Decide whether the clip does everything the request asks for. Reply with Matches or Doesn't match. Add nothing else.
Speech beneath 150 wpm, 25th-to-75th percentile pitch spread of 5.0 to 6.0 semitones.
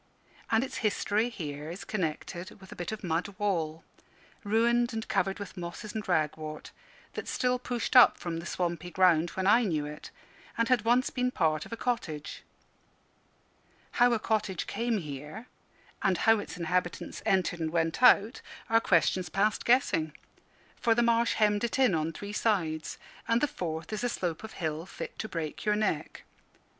Doesn't match